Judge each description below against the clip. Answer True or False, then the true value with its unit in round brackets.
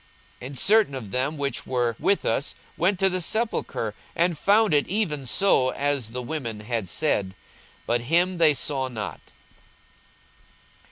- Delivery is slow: False (155 wpm)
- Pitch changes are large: True (6.5 semitones)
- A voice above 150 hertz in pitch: False (140 Hz)